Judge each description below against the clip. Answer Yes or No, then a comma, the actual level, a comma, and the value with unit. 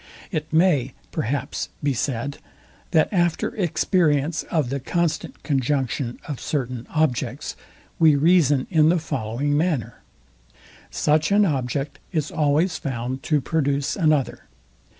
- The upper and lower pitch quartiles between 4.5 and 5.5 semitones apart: No, average, 3.3 semitones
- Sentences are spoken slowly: Yes, slow, 120 wpm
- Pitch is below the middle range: No, medium, 145 Hz